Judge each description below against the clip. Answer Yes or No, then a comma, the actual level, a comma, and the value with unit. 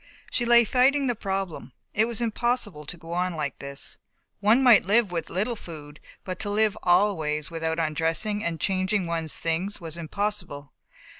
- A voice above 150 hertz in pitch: Yes, medium, 185 Hz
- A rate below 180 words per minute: Yes, average, 165 wpm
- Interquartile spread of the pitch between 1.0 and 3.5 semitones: No, average, 4.7 semitones